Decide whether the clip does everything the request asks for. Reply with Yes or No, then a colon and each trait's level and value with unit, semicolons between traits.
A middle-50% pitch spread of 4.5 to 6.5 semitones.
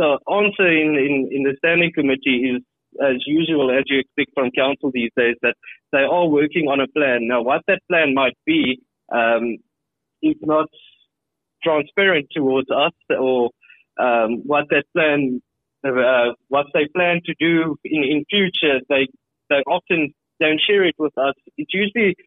No: average, 3.7 semitones